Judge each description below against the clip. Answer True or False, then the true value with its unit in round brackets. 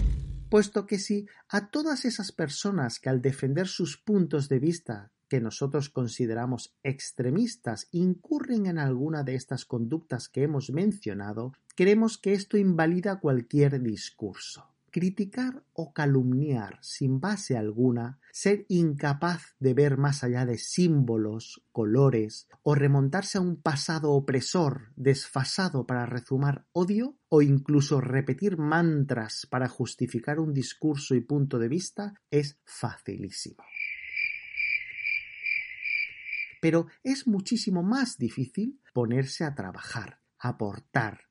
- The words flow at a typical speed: False (120 wpm)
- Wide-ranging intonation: True (7.3 semitones)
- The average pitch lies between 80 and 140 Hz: False (150 Hz)